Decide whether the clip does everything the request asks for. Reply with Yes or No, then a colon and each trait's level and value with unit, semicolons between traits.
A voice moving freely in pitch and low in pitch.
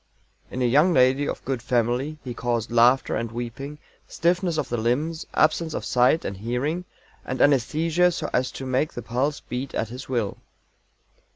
No: average, 4.0 semitones; low, 130 Hz